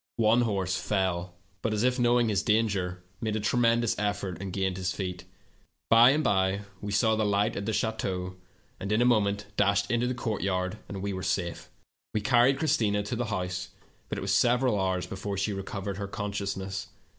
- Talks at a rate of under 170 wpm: No, average, 190 wpm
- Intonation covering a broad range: No, average, 2.9 semitones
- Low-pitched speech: Yes, low, 100 Hz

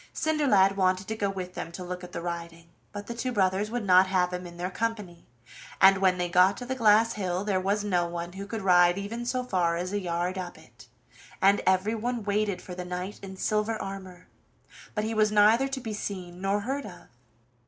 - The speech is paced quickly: Yes, fast, 215 wpm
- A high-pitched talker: Yes, high, 195 Hz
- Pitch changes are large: No, average, 2.9 semitones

